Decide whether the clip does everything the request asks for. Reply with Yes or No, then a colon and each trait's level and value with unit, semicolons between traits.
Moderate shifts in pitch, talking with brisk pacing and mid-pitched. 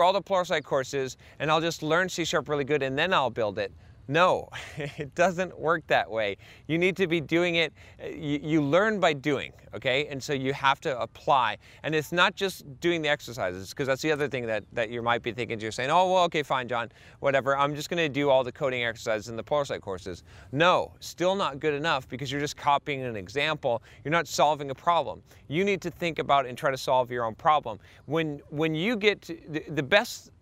Yes: average, 5.0 semitones; fast, 225 wpm; medium, 145 Hz